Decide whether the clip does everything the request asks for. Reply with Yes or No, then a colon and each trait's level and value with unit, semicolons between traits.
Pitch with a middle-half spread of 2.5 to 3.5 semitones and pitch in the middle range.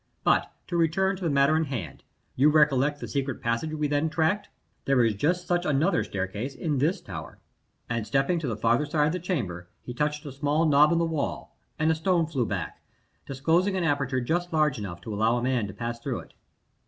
No: average, 5.1 semitones; medium, 145 Hz